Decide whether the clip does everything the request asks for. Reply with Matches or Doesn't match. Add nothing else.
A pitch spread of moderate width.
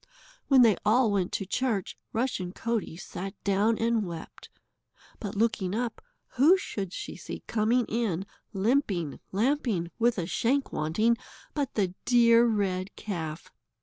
Matches